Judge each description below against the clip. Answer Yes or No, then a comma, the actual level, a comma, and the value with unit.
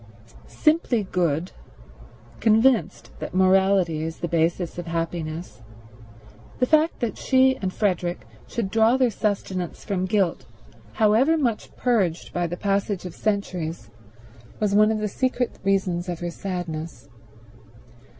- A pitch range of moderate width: Yes, average, 4.2 semitones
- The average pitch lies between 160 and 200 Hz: Yes, high, 190 Hz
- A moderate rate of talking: No, slow, 130 wpm